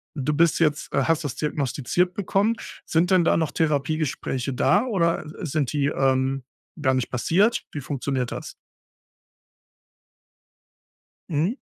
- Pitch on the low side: No, medium, 150 Hz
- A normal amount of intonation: Yes, average, 3.7 semitones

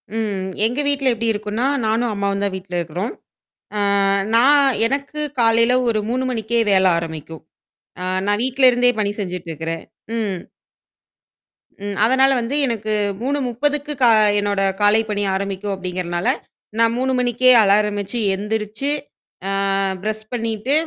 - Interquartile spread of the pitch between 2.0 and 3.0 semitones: No, average, 3.8 semitones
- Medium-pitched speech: No, high, 220 Hz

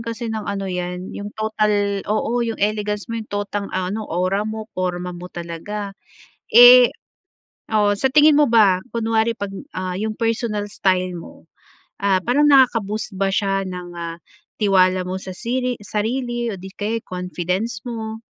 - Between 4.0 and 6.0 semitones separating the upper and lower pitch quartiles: No, average, 3.5 semitones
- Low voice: No, high, 205 Hz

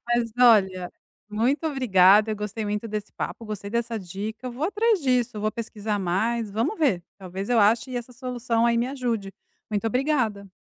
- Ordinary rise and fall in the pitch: Yes, average, 3.2 semitones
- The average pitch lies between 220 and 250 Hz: Yes, high, 225 Hz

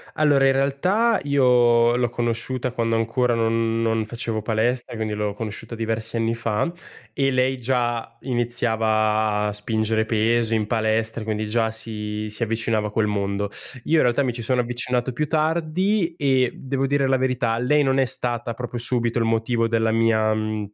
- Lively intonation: No, narrow, 2.5 semitones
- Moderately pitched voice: No, low, 115 Hz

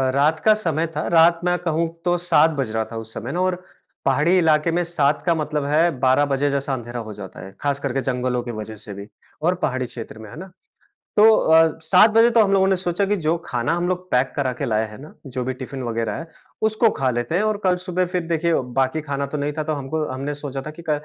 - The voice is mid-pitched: Yes, medium, 150 Hz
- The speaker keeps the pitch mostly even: No, average, 5.2 semitones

